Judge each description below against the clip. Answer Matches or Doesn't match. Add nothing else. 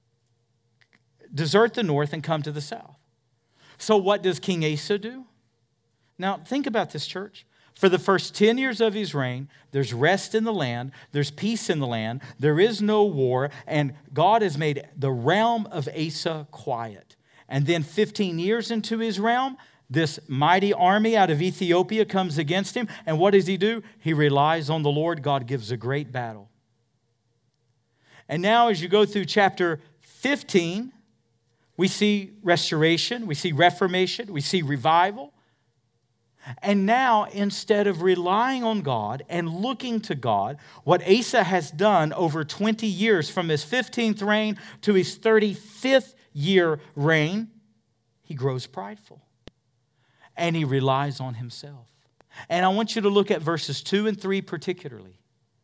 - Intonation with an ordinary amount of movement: Doesn't match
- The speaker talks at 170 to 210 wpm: Doesn't match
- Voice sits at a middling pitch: Matches